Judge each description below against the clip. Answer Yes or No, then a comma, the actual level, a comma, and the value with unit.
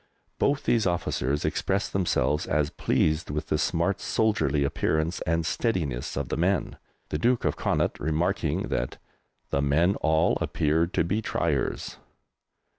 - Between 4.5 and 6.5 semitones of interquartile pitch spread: No, average, 4.0 semitones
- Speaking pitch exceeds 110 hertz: No, very low, 80 Hz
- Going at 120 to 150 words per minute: Yes, average, 140 wpm